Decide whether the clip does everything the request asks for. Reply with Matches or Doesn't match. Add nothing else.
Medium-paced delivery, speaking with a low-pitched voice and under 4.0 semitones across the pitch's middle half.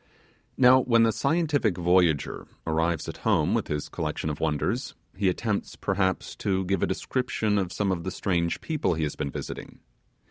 Doesn't match